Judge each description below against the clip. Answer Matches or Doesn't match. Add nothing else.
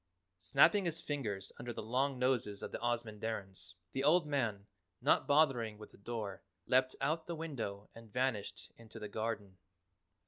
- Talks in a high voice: Doesn't match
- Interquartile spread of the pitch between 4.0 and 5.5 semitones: Matches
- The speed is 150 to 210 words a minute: Matches